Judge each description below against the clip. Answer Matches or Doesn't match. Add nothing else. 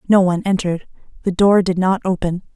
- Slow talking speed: Doesn't match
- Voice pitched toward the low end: Doesn't match